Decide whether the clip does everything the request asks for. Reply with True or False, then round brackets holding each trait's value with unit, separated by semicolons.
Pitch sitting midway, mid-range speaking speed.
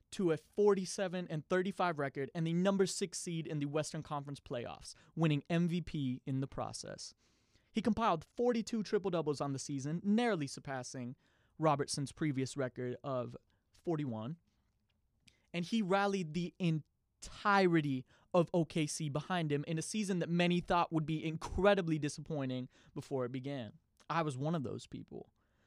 True (160 Hz; 150 wpm)